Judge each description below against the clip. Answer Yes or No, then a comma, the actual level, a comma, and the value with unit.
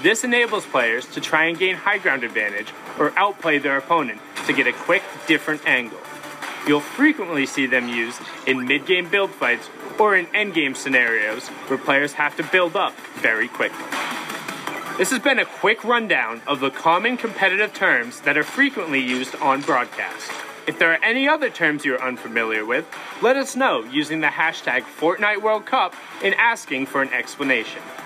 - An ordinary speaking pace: Yes, average, 175 wpm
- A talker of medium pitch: Yes, medium, 165 Hz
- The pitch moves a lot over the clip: Yes, wide, 7.4 semitones